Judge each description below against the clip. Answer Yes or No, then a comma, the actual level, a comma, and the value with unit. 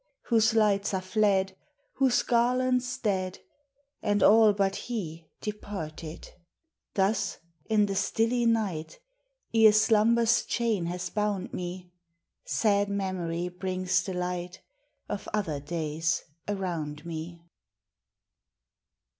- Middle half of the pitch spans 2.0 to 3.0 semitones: No, average, 3.6 semitones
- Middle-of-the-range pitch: No, high, 195 Hz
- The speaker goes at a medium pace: No, slow, 105 wpm